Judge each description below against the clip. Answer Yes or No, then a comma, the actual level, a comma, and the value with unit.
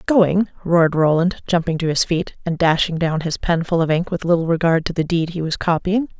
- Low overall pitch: No, medium, 170 Hz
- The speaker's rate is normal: No, fast, 230 wpm